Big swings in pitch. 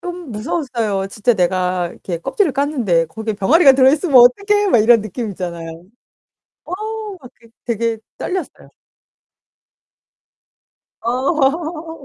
Yes: wide, 7.4 semitones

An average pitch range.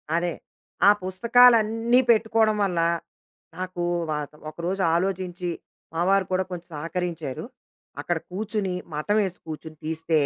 Yes: average, 3.7 semitones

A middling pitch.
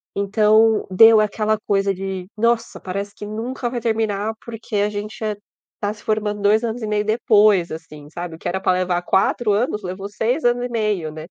No: high, 210 Hz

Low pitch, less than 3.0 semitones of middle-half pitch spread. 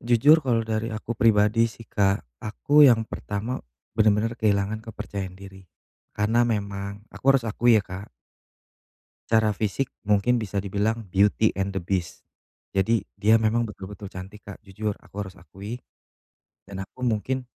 Yes: low, 105 Hz; narrow, 2.5 semitones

